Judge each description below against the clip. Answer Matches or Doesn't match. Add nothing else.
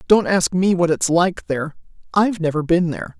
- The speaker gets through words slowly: Doesn't match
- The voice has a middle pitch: Matches